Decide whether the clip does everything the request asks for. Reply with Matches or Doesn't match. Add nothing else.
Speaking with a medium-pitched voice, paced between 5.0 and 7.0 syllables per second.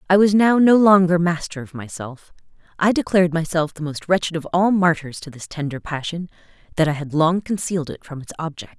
Matches